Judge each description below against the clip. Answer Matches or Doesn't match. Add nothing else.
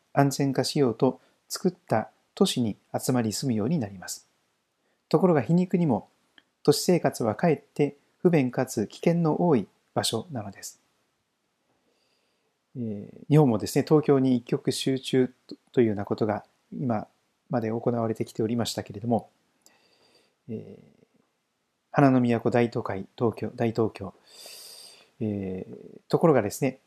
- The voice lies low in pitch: Matches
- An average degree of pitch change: Matches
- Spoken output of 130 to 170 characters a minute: Doesn't match